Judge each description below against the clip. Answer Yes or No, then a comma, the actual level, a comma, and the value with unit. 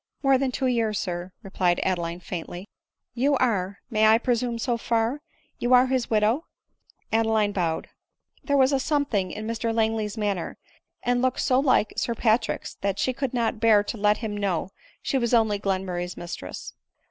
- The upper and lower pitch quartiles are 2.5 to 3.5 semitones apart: No, average, 3.9 semitones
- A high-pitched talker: Yes, high, 225 Hz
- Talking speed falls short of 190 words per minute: No, average, 195 wpm